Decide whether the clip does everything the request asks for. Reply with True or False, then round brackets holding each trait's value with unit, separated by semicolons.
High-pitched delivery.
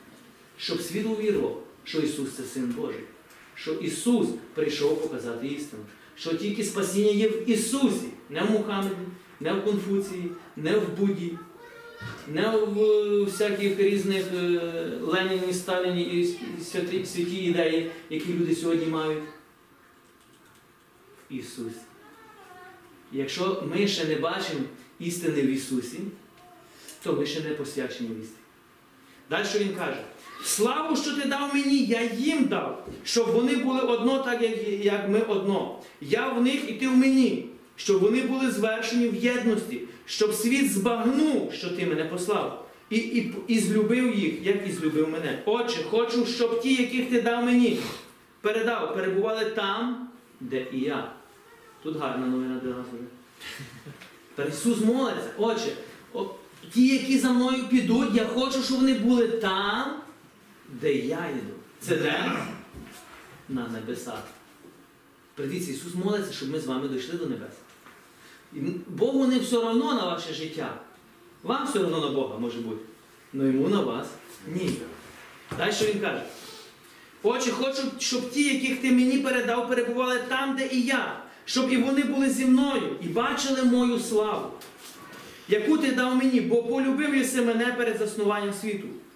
True (215 Hz)